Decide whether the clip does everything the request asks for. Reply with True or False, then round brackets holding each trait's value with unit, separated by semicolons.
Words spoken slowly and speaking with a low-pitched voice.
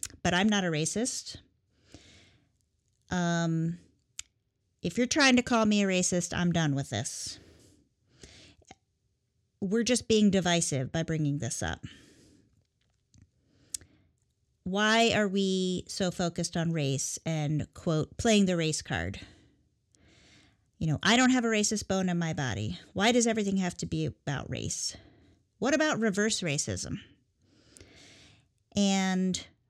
False (125 wpm; 155 Hz)